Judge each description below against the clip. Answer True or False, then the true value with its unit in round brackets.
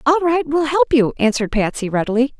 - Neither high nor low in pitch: False (260 Hz)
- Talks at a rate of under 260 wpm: True (200 wpm)